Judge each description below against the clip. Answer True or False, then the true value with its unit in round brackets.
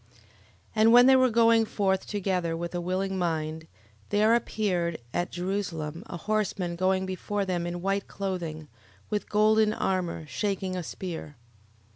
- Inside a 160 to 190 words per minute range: False (150 wpm)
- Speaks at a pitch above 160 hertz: True (190 Hz)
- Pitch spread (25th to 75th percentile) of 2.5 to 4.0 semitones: True (3.3 semitones)